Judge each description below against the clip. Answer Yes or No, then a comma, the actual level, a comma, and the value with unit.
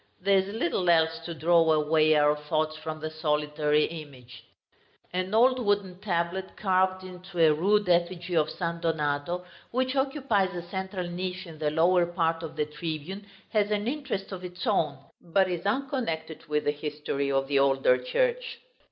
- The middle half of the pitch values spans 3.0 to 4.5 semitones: Yes, average, 3.6 semitones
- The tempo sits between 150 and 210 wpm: Yes, average, 170 wpm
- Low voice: No, medium, 170 Hz